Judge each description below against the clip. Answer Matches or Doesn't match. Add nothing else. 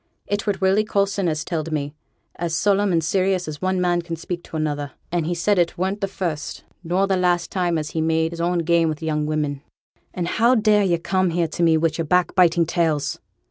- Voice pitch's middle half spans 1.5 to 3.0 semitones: Matches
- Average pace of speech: Doesn't match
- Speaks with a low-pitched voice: Doesn't match